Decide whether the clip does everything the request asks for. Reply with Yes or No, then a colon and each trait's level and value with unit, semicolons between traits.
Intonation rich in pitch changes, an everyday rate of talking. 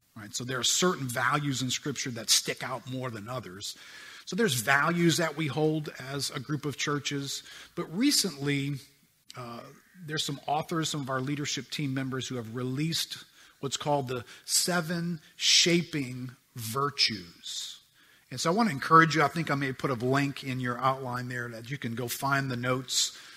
No: average, 3.4 semitones; average, 180 wpm